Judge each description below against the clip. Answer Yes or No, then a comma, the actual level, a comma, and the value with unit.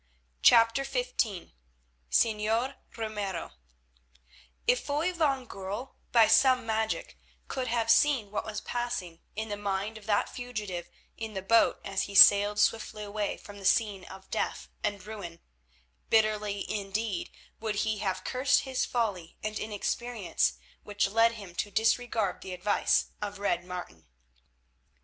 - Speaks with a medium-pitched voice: No, high, 215 Hz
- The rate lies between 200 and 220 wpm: No, average, 140 wpm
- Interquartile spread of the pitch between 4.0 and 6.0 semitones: No, narrow, 2.6 semitones